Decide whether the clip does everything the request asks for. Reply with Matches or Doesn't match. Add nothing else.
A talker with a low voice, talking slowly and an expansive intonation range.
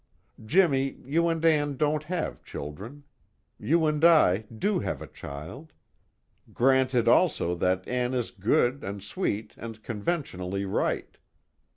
Matches